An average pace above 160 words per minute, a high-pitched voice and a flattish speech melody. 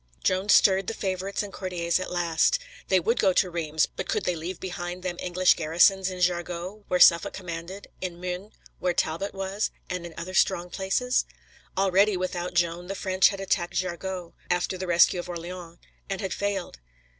No: average, 180 wpm; medium, 180 Hz; narrow, 1.7 semitones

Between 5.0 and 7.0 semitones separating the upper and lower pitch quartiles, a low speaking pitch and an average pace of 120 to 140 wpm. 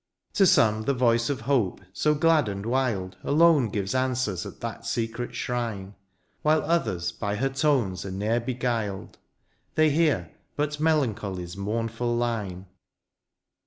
Yes: wide, 5.5 semitones; low, 120 Hz; slow, 135 wpm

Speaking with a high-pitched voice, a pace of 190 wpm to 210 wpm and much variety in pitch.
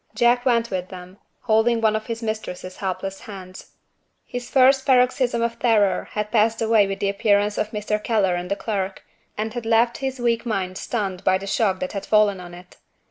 No: high, 215 Hz; average, 195 wpm; average, 3.2 semitones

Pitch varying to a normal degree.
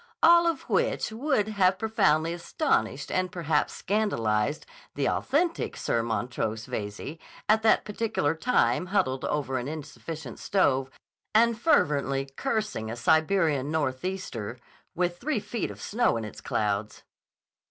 No: wide, 8.6 semitones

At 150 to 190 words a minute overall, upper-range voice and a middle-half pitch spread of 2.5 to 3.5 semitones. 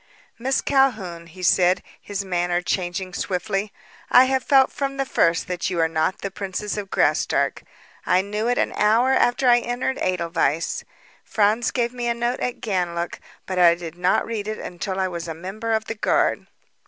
No: average, 185 wpm; high, 195 Hz; average, 5.1 semitones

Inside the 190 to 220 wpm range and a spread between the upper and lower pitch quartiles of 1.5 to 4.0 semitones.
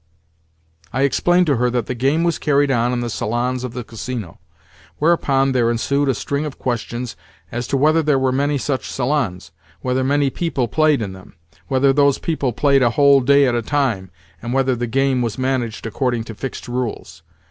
Yes: average, 195 wpm; average, 2.9 semitones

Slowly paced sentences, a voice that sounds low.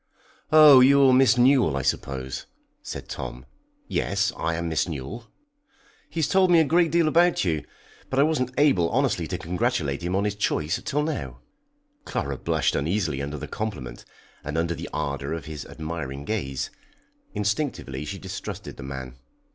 No: average, 165 wpm; very low, 90 Hz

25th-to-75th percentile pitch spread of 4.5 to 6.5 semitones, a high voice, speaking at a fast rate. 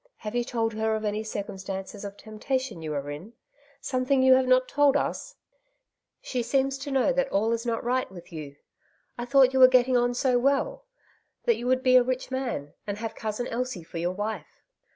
No: average, 3.7 semitones; high, 245 Hz; fast, 210 wpm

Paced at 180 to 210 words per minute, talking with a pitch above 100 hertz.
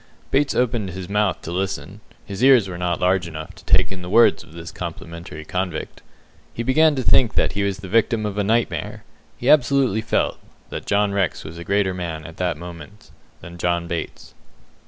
No: average, 200 wpm; very low, 95 Hz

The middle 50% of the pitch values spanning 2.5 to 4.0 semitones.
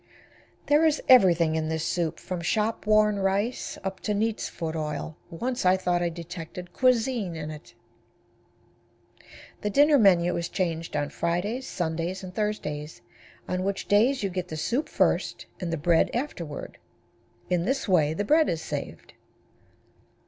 No: average, 4.5 semitones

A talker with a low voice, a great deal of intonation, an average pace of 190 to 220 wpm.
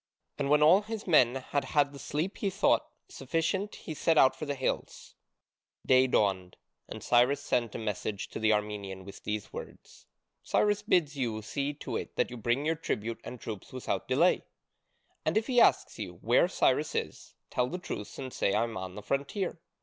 Yes: low, 130 Hz; wide, 6.3 semitones; average, 195 wpm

